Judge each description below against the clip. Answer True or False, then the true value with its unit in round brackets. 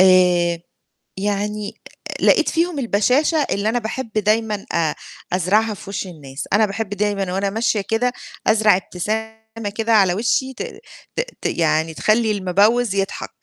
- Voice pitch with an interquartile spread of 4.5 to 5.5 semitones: False (2.9 semitones)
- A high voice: True (210 Hz)